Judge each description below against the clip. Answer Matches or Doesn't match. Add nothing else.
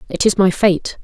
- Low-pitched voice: Doesn't match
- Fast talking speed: Matches